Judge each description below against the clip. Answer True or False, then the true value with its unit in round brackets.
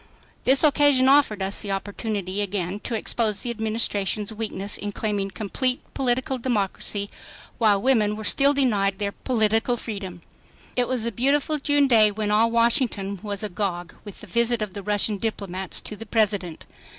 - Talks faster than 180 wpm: False (165 wpm)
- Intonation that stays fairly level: False (3.2 semitones)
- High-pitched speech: True (215 Hz)